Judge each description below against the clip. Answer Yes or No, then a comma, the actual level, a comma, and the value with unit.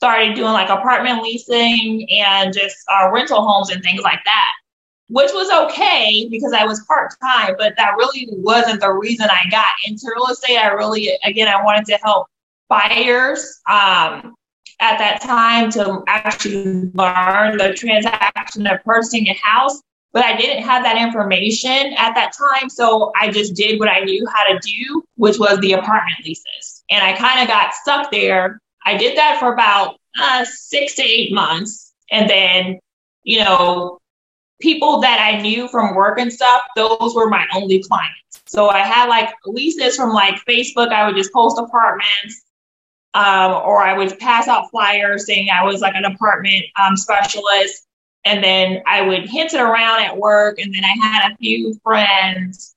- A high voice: Yes, high, 215 Hz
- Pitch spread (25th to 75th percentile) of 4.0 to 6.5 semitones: No, average, 3.4 semitones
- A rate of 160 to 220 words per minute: Yes, average, 175 wpm